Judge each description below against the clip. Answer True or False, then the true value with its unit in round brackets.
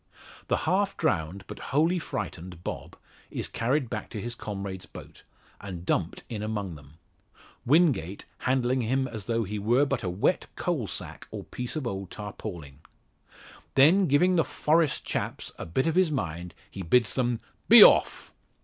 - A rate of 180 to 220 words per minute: False (165 wpm)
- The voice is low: True (115 Hz)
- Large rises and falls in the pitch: True (6.5 semitones)